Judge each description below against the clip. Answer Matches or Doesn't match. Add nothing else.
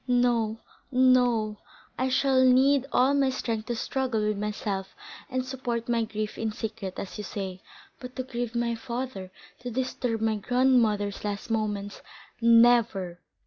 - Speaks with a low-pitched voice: Doesn't match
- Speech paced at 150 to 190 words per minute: Doesn't match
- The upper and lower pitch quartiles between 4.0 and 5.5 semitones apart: Doesn't match